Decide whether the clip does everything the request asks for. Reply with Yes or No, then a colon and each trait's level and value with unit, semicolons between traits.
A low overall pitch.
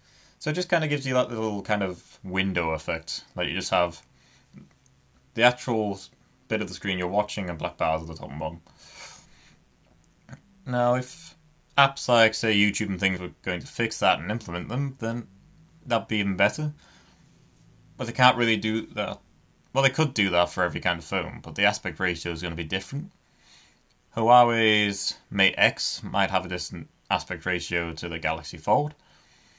Yes: low, 105 Hz